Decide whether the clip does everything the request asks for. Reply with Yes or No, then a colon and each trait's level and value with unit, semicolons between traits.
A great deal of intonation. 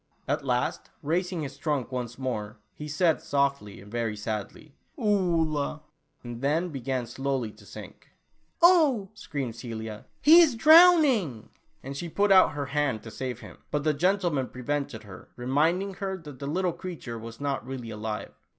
Yes: wide, 6.9 semitones